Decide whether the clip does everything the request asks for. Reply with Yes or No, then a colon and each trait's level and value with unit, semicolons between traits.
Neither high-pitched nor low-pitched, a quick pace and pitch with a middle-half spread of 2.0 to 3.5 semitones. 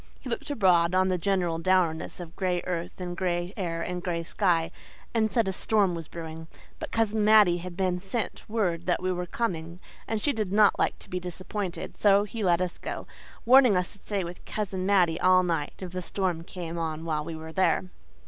Yes: medium, 180 Hz; fast, 210 wpm; average, 2.8 semitones